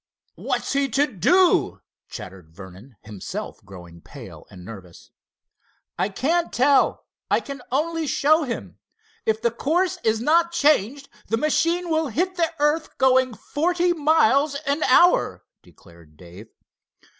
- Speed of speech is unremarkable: No, slow, 130 wpm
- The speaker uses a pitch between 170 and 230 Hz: No, very high, 275 Hz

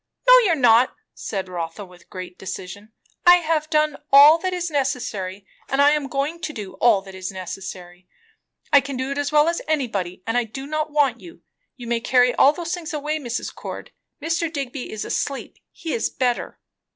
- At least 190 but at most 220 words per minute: Yes, average, 200 wpm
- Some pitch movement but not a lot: No, wide, 6.9 semitones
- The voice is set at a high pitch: Yes, very high, 270 Hz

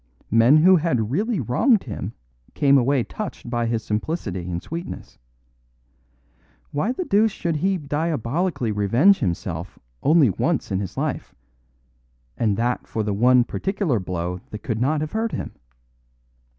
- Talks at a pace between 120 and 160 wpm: Yes, average, 145 wpm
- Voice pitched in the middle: No, low, 130 Hz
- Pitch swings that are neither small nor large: No, wide, 7.9 semitones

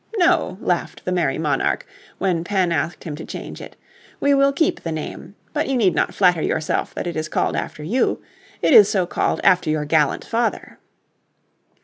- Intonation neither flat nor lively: No, wide, 6.3 semitones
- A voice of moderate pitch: Yes, medium, 180 Hz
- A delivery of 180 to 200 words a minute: Yes, average, 190 wpm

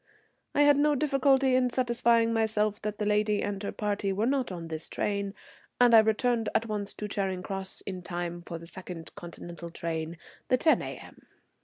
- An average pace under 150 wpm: No, average, 185 wpm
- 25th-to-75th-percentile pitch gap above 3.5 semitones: Yes, average, 4.5 semitones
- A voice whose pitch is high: Yes, high, 210 Hz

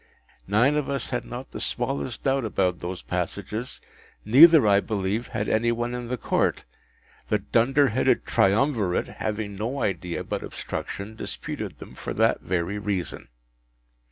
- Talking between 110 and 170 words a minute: Yes, average, 150 wpm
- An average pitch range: Yes, average, 4.0 semitones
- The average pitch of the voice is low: Yes, low, 110 Hz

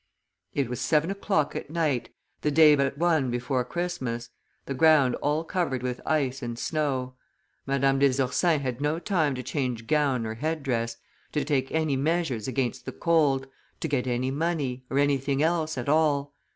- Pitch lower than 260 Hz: Yes, medium, 140 Hz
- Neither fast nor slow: Yes, average, 180 wpm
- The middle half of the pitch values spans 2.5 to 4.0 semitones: Yes, average, 3.5 semitones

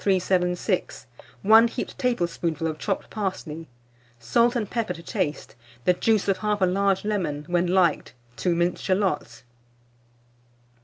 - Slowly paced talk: Yes, slow, 125 wpm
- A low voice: No, medium, 185 Hz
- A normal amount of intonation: Yes, average, 3.4 semitones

